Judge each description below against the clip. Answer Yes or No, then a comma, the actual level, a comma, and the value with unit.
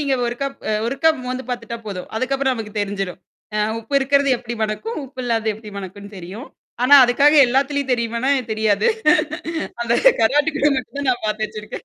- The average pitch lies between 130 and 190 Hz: No, high, 240 Hz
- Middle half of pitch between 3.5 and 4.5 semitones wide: Yes, average, 4.2 semitones